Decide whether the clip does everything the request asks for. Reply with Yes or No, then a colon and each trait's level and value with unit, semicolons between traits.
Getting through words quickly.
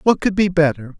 Yes: fast, 240 wpm